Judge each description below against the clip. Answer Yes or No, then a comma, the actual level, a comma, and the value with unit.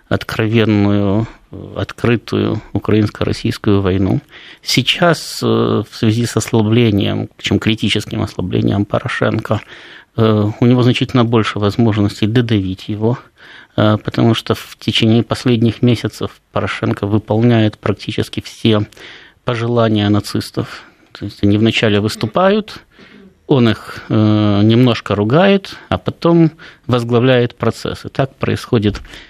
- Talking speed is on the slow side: Yes, slow, 95 wpm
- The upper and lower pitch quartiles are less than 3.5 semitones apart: Yes, narrow, 2.4 semitones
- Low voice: Yes, low, 115 Hz